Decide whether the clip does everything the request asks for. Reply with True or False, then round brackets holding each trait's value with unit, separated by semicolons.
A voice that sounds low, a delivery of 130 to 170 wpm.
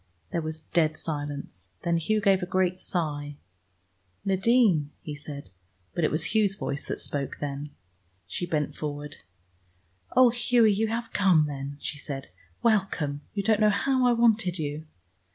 False (165 Hz; 155 wpm)